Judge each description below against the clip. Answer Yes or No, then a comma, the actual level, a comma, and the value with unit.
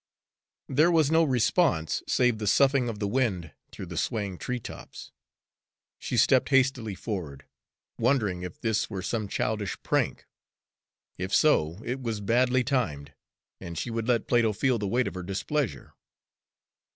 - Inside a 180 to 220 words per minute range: No, average, 150 wpm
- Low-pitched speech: Yes, low, 115 Hz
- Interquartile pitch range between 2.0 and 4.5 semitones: No, average, 5.1 semitones